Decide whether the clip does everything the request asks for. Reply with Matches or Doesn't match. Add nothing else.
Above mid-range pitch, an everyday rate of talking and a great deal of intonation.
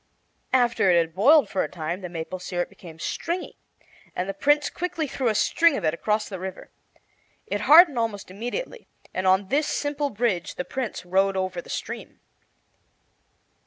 Matches